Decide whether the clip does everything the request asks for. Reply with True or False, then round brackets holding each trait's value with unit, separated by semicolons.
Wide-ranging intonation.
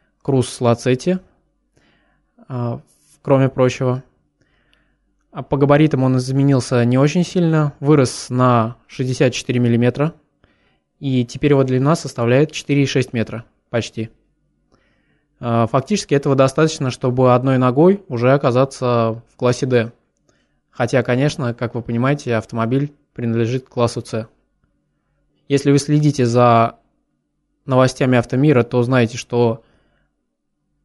False (2.8 semitones)